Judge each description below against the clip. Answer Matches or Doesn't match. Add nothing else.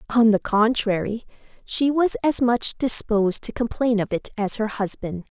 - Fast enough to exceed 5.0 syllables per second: Doesn't match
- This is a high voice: Matches